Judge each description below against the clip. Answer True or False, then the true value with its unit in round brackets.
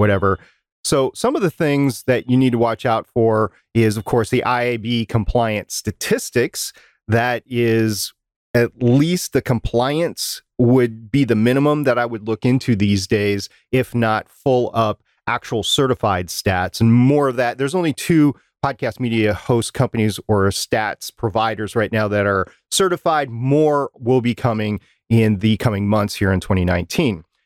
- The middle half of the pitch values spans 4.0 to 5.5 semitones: False (3.1 semitones)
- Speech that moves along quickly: False (160 wpm)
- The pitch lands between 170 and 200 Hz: False (115 Hz)